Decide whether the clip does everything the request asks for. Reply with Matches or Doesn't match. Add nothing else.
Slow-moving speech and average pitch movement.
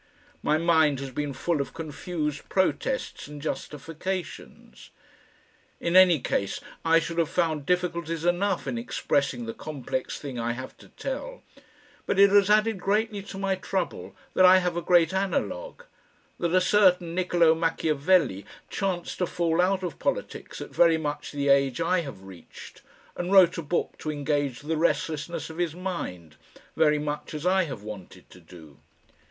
Doesn't match